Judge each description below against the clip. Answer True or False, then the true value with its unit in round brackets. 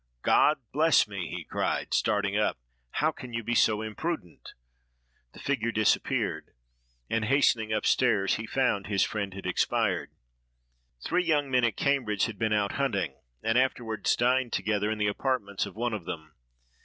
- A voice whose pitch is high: False (110 Hz)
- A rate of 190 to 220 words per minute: False (165 wpm)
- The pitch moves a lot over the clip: False (3.6 semitones)